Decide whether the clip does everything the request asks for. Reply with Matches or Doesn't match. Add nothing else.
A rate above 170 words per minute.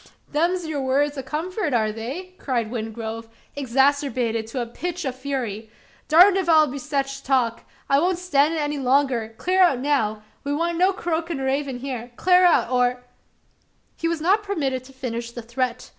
Matches